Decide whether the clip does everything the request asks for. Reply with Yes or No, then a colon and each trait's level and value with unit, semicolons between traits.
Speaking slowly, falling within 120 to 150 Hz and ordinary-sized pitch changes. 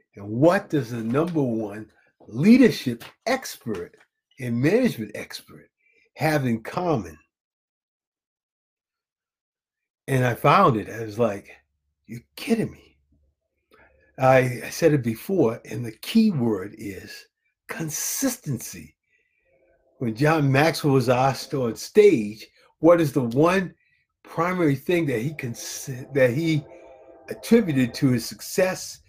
No: slow, 120 wpm; medium, 140 Hz; wide, 6.2 semitones